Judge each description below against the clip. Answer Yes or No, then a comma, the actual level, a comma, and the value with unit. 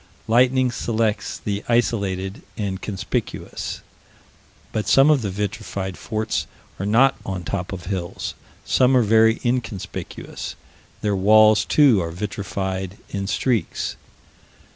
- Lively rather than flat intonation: No, average, 3.3 semitones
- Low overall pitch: Yes, low, 105 Hz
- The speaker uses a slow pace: Yes, slow, 120 wpm